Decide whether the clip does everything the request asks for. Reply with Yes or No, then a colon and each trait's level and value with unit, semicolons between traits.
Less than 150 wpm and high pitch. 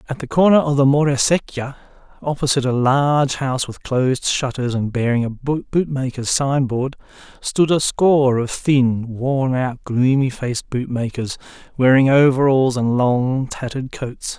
No: average, 140 wpm; low, 130 Hz